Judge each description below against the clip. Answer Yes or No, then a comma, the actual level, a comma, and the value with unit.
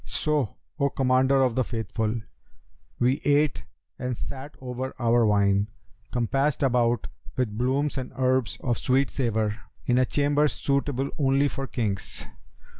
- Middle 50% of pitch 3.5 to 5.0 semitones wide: No, average, 2.8 semitones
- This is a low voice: Yes, low, 130 Hz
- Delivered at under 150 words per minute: Yes, slow, 135 wpm